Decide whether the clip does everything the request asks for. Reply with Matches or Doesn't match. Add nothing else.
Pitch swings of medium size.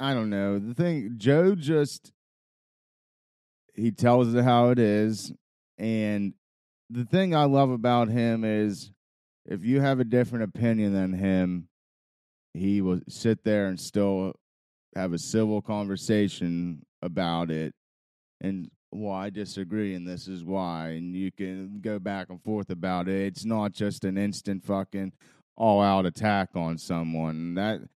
Matches